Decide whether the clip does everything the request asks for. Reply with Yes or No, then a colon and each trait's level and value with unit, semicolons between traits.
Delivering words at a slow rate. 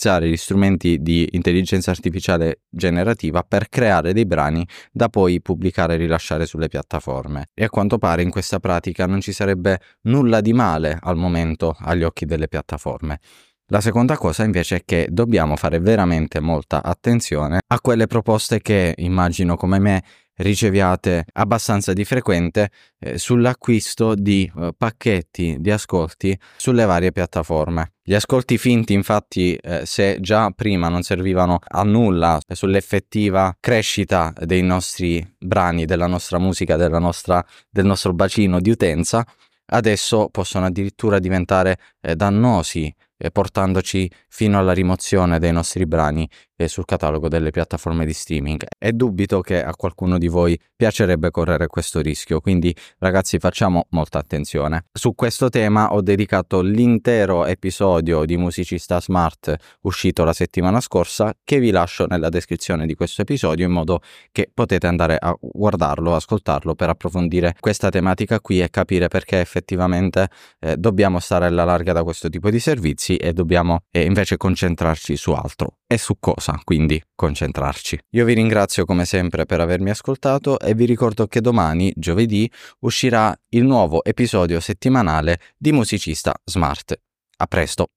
No: average, 145 wpm